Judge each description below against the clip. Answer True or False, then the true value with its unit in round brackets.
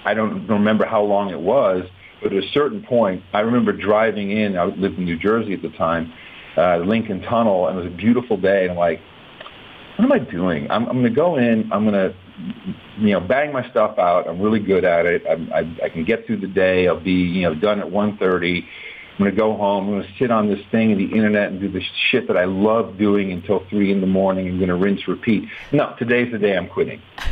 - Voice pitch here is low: True (100 Hz)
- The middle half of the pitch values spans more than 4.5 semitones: False (2.7 semitones)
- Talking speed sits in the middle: False (255 wpm)